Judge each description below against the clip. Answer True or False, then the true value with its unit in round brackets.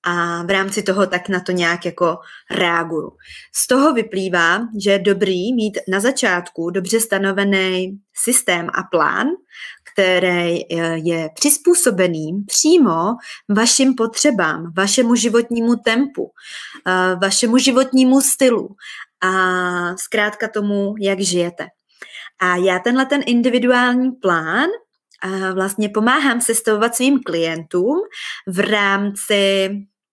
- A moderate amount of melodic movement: True (4.8 semitones)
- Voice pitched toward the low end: False (200 Hz)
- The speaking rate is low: True (110 wpm)